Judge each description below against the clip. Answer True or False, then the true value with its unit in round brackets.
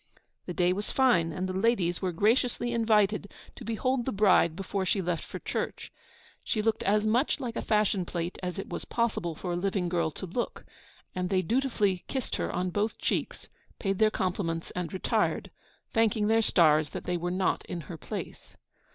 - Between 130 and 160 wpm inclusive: False (190 wpm)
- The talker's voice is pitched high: True (195 Hz)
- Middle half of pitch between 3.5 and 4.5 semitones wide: True (3.8 semitones)